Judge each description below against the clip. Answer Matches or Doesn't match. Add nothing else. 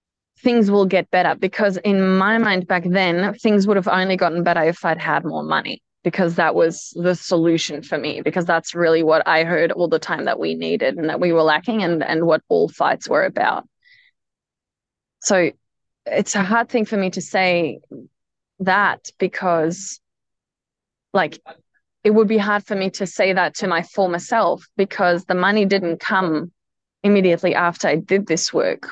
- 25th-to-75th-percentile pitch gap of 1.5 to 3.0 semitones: Doesn't match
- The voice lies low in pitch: Doesn't match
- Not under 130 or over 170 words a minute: Doesn't match